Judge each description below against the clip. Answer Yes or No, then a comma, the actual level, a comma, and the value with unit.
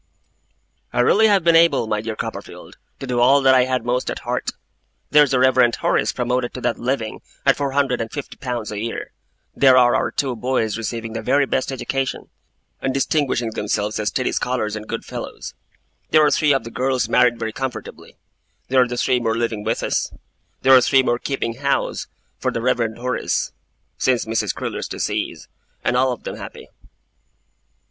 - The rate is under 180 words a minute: No, average, 185 wpm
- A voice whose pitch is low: Yes, low, 125 Hz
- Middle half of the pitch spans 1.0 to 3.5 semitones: Yes, narrow, 2.5 semitones